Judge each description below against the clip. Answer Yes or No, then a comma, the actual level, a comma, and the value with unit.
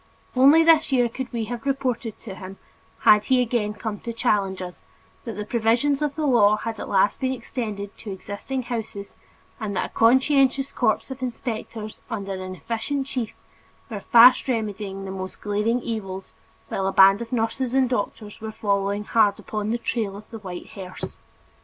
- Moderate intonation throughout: Yes, average, 3.7 semitones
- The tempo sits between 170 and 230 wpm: Yes, average, 180 wpm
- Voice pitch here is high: Yes, high, 225 Hz